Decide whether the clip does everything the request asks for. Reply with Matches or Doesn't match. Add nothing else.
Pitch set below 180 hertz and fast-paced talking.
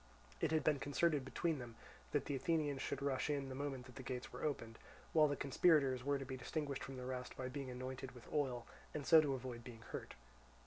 Matches